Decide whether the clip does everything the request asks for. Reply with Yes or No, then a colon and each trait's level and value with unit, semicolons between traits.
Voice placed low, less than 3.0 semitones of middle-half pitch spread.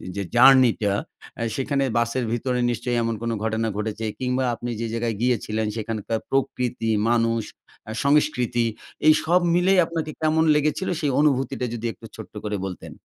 No: low, 120 Hz; average, 3.7 semitones